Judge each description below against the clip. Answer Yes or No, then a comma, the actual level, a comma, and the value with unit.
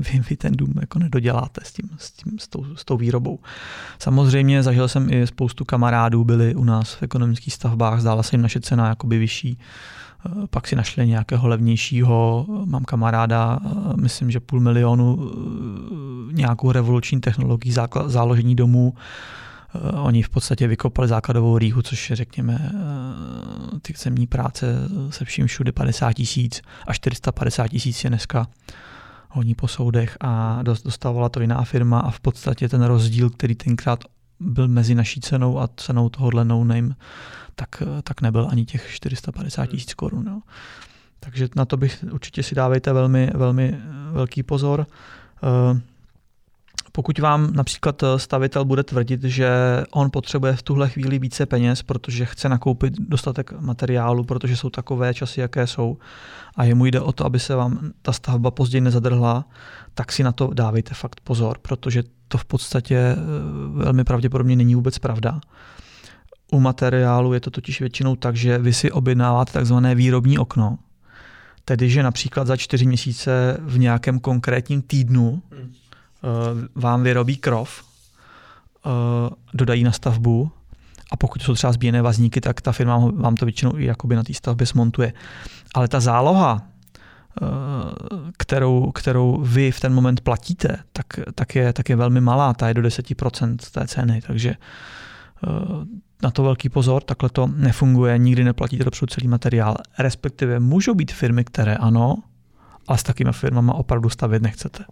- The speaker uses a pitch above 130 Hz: No, low, 125 Hz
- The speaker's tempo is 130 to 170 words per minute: Yes, average, 150 wpm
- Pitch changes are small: Yes, narrow, 2.0 semitones